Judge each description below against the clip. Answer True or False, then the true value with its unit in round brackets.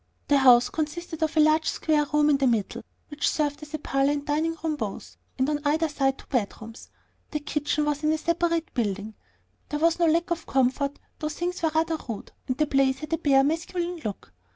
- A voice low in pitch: False (300 Hz)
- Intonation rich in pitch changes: False (2.9 semitones)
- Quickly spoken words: True (210 wpm)